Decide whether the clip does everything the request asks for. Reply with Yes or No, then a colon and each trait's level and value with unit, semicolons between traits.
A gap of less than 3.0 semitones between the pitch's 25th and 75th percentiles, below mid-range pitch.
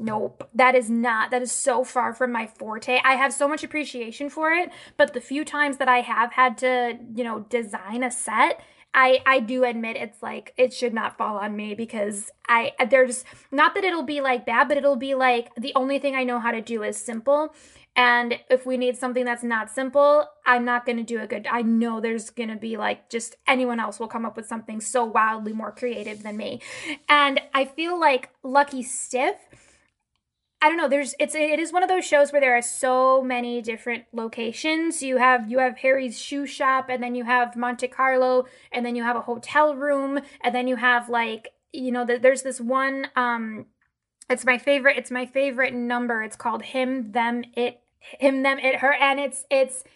No: narrow, 2.5 semitones; very high, 255 Hz